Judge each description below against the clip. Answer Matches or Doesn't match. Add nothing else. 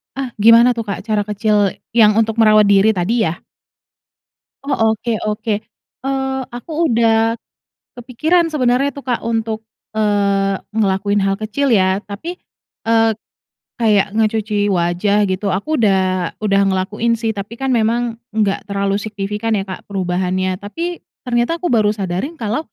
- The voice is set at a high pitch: Matches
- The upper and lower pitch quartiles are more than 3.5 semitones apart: Doesn't match